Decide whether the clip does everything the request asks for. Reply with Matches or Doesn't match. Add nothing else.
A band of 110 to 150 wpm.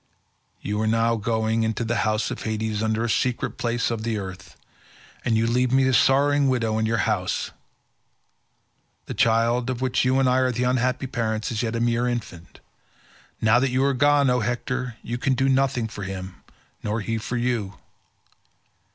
Doesn't match